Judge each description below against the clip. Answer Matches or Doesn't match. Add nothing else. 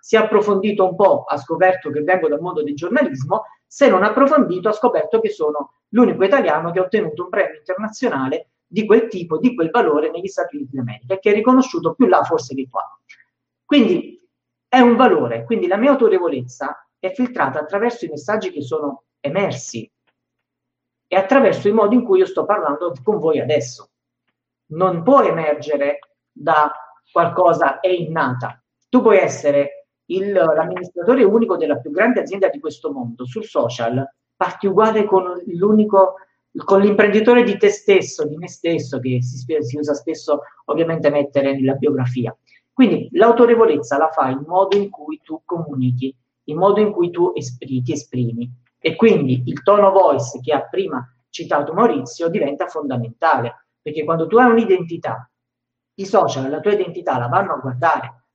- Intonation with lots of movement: Matches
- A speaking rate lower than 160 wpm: Doesn't match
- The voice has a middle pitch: Matches